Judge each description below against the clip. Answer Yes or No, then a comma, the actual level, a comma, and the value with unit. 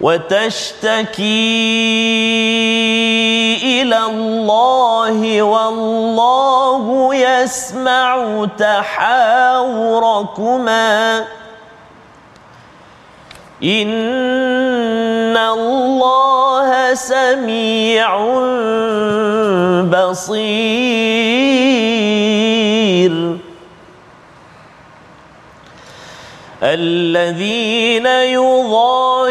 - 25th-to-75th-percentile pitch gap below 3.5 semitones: Yes, average, 2.8 semitones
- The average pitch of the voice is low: No, high, 225 Hz